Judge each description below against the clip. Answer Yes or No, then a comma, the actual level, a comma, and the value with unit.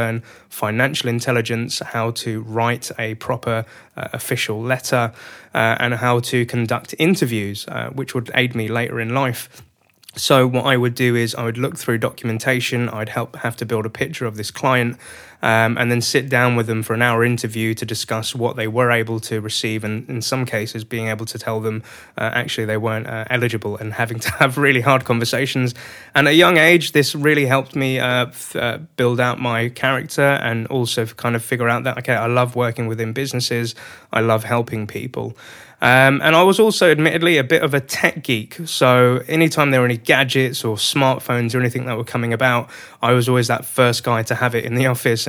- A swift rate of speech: Yes, fast, 210 wpm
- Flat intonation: Yes, narrow, 2.2 semitones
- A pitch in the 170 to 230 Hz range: No, low, 120 Hz